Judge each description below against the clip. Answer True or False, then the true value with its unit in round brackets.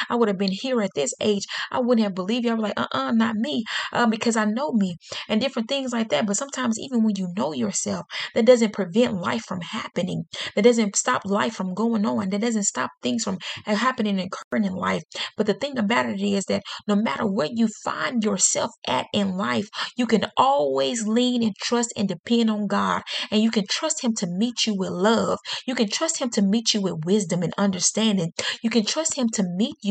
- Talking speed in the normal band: False (230 wpm)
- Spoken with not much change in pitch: False (3.0 semitones)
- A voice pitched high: True (220 Hz)